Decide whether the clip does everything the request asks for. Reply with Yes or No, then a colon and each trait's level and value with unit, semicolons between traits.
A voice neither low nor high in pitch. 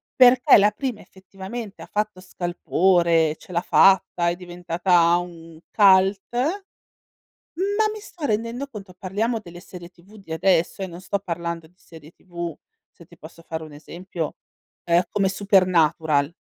Yes: medium, 180 Hz